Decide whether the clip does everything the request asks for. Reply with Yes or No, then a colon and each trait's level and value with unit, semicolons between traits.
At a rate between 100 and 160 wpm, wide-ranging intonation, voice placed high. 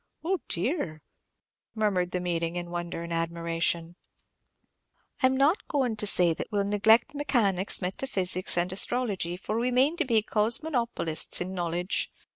Yes: average, 150 wpm; wide, 5.9 semitones; high, 195 Hz